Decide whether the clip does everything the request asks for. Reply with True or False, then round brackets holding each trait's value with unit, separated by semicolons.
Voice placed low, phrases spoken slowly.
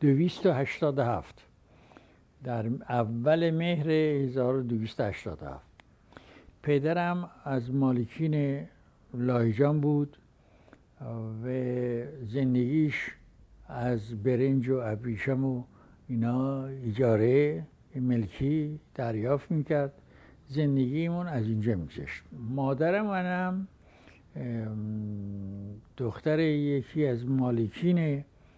True (130 Hz; 65 wpm)